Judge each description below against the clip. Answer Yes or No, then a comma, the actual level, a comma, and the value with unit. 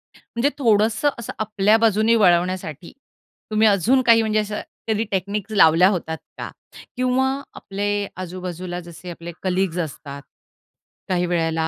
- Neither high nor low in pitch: No, high, 195 Hz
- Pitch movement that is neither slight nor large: Yes, average, 3.7 semitones